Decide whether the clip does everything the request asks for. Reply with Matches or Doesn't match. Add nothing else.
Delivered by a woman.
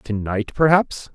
Doesn't match